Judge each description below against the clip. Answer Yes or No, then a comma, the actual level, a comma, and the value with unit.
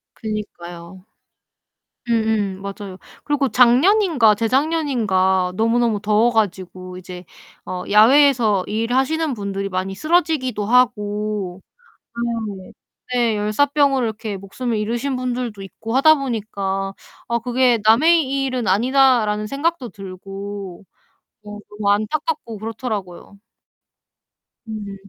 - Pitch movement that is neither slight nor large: Yes, average, 4.3 semitones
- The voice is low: No, high, 220 Hz